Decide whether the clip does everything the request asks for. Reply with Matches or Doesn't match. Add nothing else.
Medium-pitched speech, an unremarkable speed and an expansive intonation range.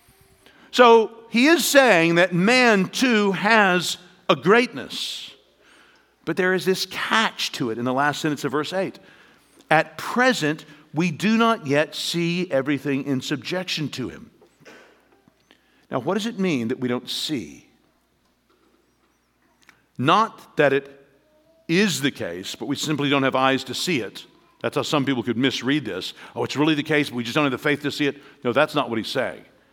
Matches